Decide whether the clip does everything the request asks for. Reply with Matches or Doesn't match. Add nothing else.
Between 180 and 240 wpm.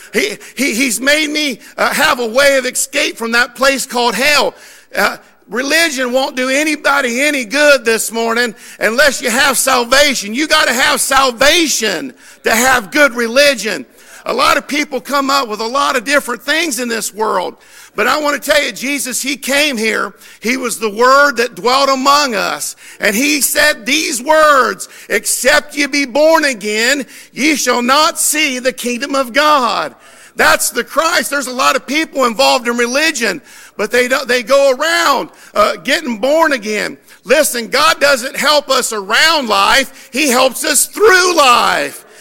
Doesn't match